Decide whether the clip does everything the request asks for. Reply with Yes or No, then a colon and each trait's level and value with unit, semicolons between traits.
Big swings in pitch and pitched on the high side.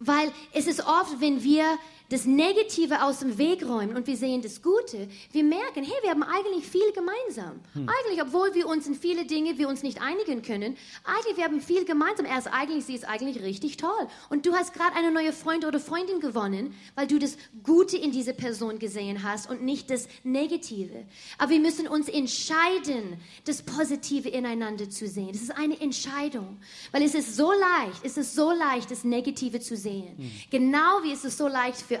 No: average, 4.7 semitones; very high, 285 Hz